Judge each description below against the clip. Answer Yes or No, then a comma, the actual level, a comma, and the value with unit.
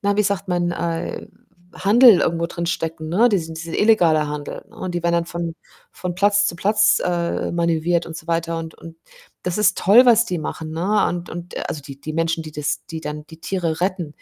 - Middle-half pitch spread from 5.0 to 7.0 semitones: No, average, 2.7 semitones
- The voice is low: No, medium, 170 Hz